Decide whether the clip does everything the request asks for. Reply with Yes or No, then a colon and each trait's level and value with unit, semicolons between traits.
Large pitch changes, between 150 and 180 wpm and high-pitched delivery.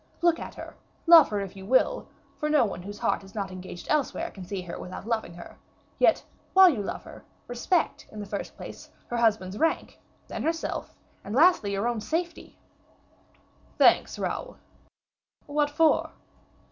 Yes: wide, 7.6 semitones; average, 170 wpm; high, 225 Hz